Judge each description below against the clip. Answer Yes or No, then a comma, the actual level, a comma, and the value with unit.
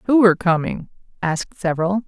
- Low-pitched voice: No, medium, 185 Hz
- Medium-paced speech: Yes, average, 145 wpm